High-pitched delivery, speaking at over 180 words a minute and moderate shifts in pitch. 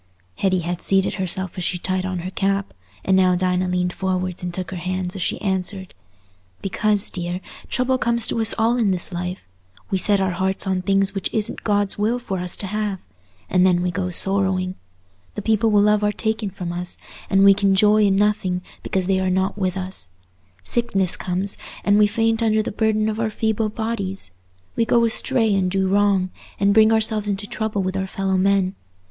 No: high, 195 Hz; fast, 205 wpm; narrow, 2.3 semitones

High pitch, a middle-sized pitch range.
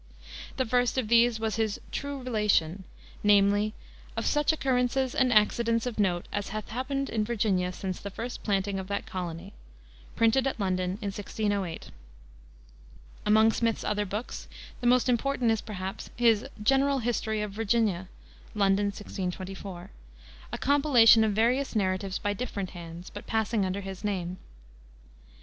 Yes: high, 210 Hz; average, 3.6 semitones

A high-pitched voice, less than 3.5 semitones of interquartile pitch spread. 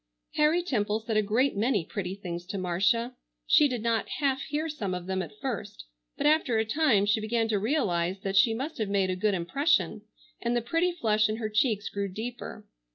No: high, 215 Hz; average, 4.7 semitones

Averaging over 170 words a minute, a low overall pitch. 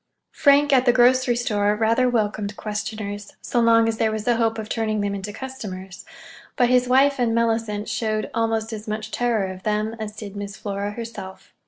No: average, 185 wpm; high, 220 Hz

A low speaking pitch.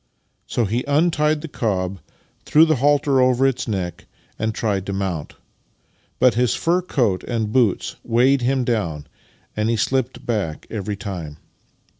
Yes: low, 115 Hz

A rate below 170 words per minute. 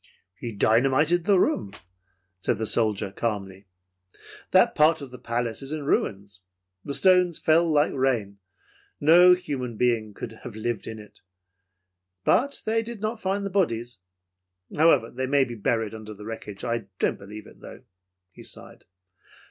Yes: average, 155 wpm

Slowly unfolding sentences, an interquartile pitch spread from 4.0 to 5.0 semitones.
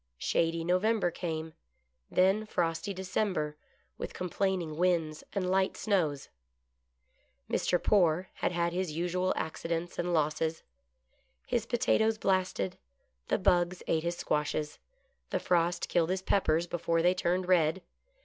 No: slow, 125 wpm; narrow, 2.4 semitones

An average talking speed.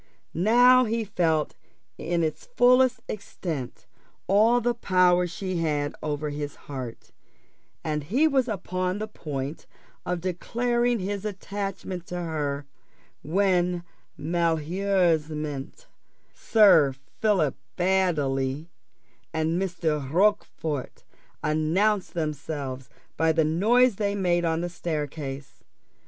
No: slow, 105 wpm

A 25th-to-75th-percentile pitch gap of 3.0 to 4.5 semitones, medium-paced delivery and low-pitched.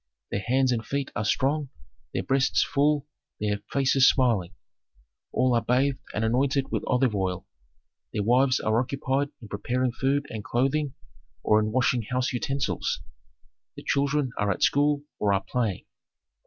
Yes: average, 4.1 semitones; average, 155 wpm; low, 125 Hz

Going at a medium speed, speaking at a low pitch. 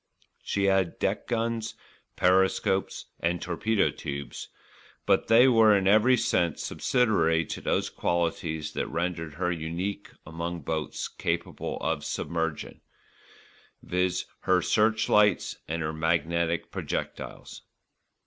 No: slow, 110 wpm; very low, 85 Hz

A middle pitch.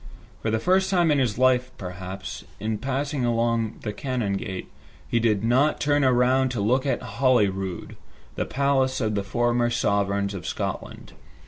No: low, 120 Hz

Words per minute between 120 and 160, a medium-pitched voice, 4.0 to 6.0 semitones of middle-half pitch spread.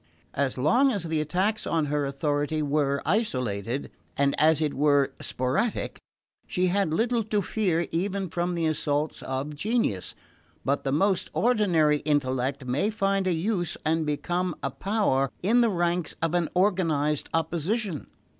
Yes: average, 150 wpm; medium, 160 Hz; average, 5.1 semitones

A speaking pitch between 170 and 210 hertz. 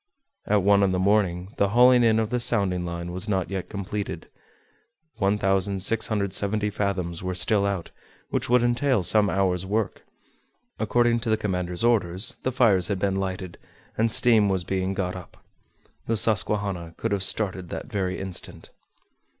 No: low, 100 Hz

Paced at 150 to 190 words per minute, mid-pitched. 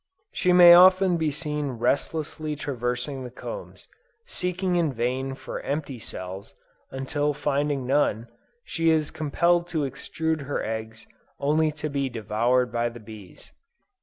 No: slow, 135 wpm; medium, 145 Hz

